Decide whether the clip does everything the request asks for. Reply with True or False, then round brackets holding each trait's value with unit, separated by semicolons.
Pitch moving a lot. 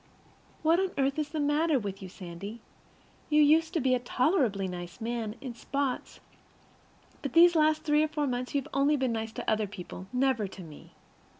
True (5.9 semitones)